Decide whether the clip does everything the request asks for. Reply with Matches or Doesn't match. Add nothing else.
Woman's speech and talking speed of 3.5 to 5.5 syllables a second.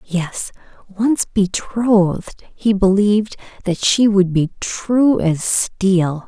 Doesn't match